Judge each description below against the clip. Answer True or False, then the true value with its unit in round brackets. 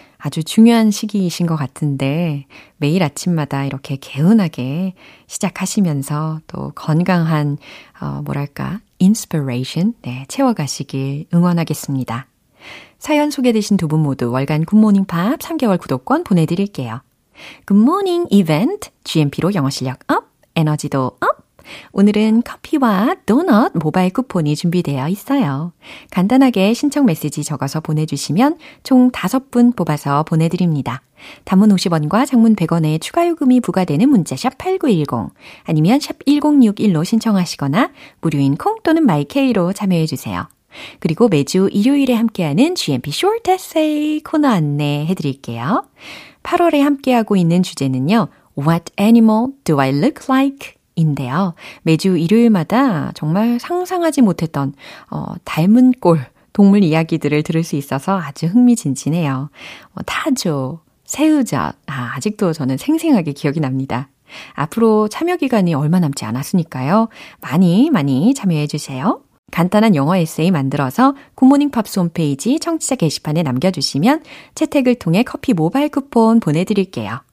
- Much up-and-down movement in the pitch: True (8.6 semitones)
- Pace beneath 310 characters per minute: False (320 characters per minute)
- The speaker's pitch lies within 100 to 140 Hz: False (180 Hz)